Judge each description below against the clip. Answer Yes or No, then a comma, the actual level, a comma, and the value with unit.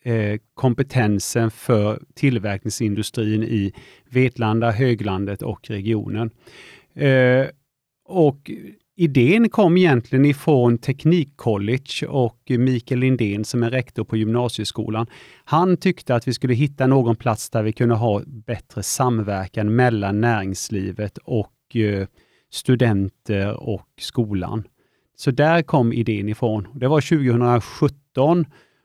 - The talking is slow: Yes, slow, 105 wpm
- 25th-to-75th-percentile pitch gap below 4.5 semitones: Yes, average, 3.8 semitones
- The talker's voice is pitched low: Yes, low, 120 Hz